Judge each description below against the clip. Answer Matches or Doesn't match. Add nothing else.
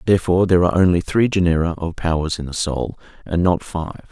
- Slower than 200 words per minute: Doesn't match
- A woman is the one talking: Doesn't match